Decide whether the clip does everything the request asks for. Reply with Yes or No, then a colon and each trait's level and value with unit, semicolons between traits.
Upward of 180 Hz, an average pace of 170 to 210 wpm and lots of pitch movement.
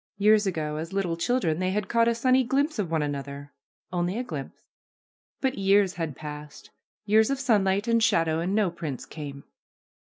Yes: high, 190 Hz; average, 180 wpm; wide, 5.9 semitones